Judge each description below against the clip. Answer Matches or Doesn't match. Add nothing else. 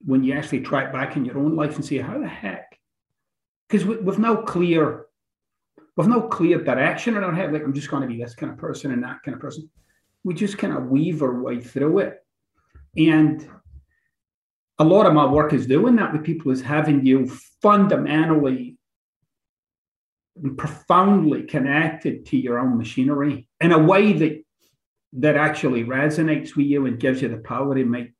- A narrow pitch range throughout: Doesn't match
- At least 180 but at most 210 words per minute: Matches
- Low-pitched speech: Doesn't match